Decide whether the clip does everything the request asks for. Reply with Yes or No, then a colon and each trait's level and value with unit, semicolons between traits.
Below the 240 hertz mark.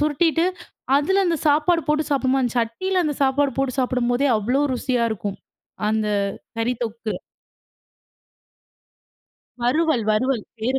No: very high, 265 Hz